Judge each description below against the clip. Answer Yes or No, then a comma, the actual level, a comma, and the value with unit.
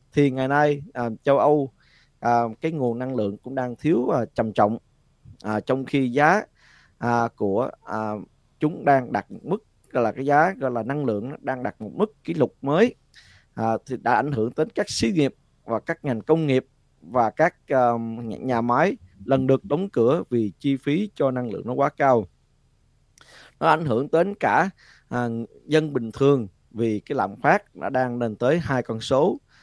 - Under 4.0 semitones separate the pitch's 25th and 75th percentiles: Yes, average, 3.5 semitones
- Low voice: Yes, low, 130 Hz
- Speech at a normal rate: Yes, average, 195 wpm